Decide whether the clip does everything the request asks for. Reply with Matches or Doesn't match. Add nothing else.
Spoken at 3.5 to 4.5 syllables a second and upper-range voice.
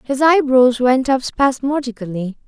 Matches